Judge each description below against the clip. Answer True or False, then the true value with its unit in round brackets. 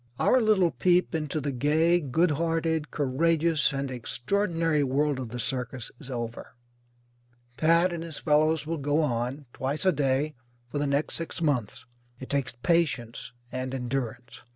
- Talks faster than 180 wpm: False (155 wpm)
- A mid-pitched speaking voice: True (145 Hz)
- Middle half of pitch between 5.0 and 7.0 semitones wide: False (4.0 semitones)